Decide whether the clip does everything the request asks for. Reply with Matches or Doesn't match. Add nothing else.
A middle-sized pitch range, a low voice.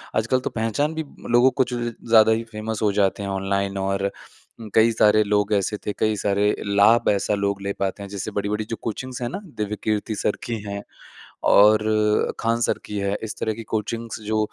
Doesn't match